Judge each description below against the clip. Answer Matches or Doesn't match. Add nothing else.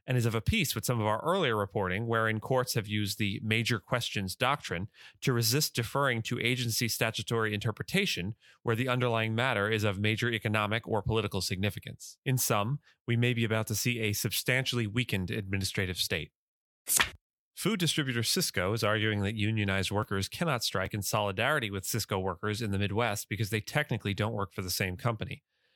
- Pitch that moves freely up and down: Doesn't match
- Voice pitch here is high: Doesn't match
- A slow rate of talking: Doesn't match